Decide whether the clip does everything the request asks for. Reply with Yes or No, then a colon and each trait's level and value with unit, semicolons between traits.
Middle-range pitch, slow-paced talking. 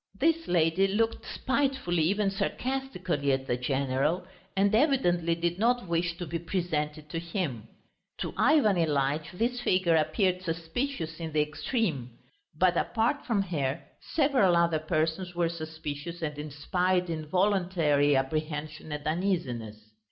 Yes: medium, 170 Hz; slow, 130 wpm